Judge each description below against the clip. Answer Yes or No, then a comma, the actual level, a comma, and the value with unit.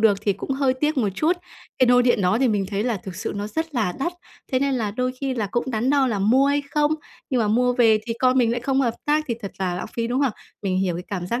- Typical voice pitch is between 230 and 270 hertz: Yes, high, 240 Hz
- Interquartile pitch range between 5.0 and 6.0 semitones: No, average, 4.3 semitones